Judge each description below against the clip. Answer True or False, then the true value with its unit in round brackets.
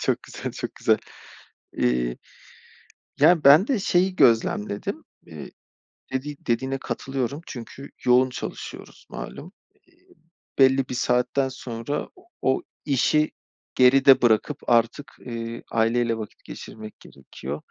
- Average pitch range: True (3.2 semitones)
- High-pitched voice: False (125 Hz)